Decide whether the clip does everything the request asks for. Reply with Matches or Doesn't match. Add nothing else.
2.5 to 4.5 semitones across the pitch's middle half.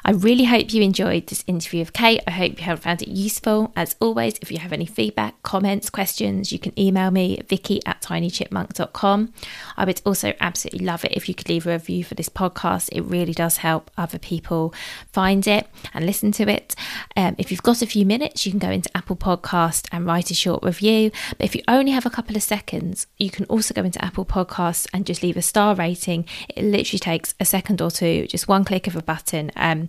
Matches